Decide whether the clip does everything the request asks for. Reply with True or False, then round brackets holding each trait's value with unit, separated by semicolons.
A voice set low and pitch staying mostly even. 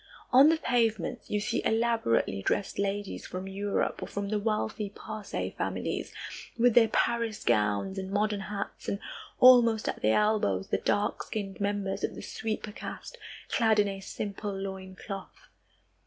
False (205 Hz; 2.3 semitones)